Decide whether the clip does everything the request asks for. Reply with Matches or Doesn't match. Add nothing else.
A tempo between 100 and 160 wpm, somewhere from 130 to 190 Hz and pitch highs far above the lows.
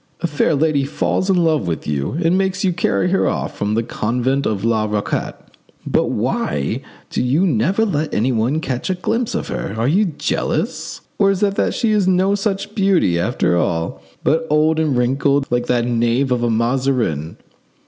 Doesn't match